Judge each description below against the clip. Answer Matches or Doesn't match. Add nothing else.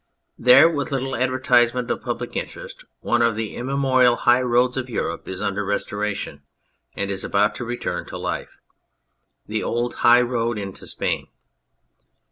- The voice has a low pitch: Matches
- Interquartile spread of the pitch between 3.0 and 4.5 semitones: Matches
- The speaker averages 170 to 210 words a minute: Doesn't match